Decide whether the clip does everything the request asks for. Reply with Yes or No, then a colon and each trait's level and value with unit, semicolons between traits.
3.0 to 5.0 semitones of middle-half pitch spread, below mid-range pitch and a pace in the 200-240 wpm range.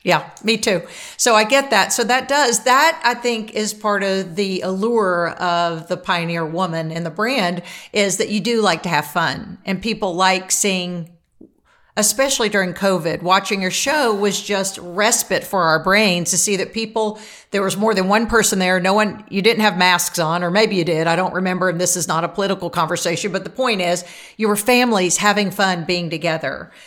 No: average, 3.4 semitones; high, 195 Hz; fast, 205 wpm